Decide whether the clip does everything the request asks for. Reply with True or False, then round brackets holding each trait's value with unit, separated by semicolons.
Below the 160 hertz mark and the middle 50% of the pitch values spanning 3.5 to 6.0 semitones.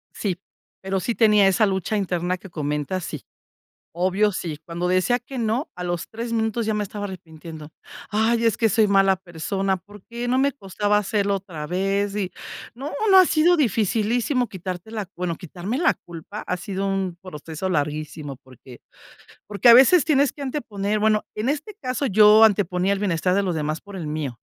False (195 Hz; 3.9 semitones)